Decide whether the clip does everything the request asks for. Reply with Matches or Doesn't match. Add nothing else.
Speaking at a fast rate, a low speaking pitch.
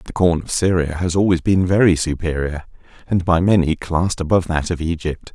Doesn't match